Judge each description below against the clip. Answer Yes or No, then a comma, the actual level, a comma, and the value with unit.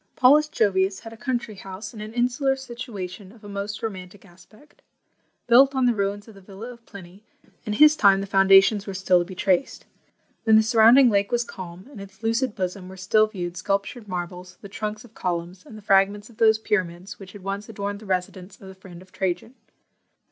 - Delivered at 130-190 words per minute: No, fast, 205 wpm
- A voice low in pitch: No, high, 200 Hz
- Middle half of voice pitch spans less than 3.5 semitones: Yes, average, 3.0 semitones